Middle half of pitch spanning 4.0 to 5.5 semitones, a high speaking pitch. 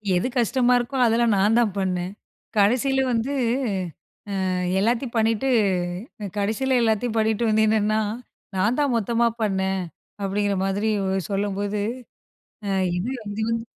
No: average, 2.9 semitones; high, 220 Hz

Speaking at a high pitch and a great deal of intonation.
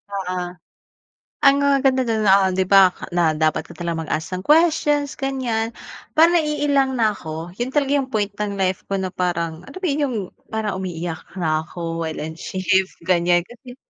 Yes: high, 195 Hz; wide, 7.2 semitones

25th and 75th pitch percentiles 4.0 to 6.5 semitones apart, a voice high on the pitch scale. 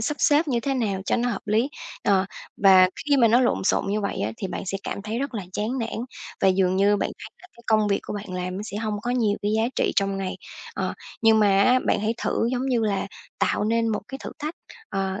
No: average, 3.4 semitones; high, 215 Hz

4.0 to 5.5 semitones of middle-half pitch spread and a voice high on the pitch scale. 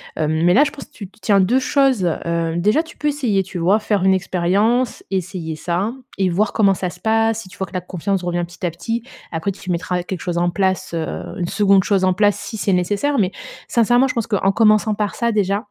No: average, 3.6 semitones; high, 195 Hz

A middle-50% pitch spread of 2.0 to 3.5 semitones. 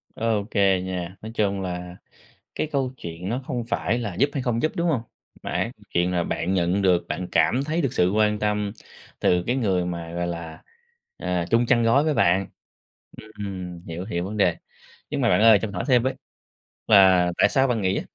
No: average, 4.7 semitones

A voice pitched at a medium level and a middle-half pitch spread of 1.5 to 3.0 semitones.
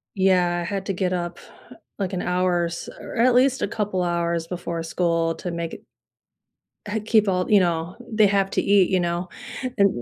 Yes: medium, 180 Hz; narrow, 2.5 semitones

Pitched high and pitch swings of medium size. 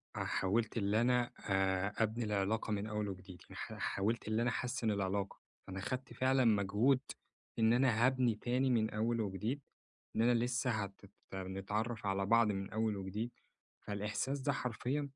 No: low, 110 Hz; average, 3.5 semitones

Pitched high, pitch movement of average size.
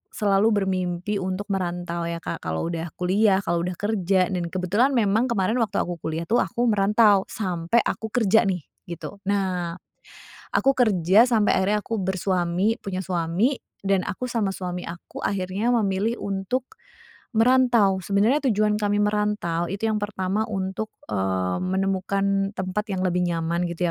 Yes: high, 195 Hz; average, 3.0 semitones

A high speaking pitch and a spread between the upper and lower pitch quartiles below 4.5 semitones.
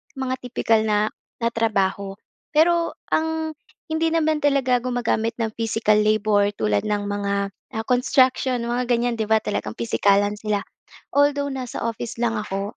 Yes: high, 230 Hz; average, 3.8 semitones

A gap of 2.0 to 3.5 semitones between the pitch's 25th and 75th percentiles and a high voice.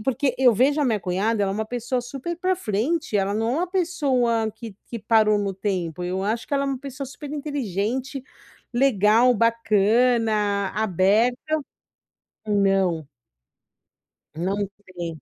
No: average, 4.7 semitones; high, 225 Hz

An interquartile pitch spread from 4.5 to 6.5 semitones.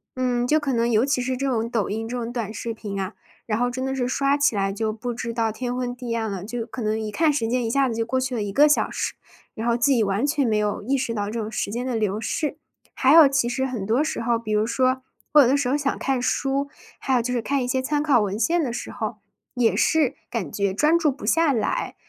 No: average, 3.2 semitones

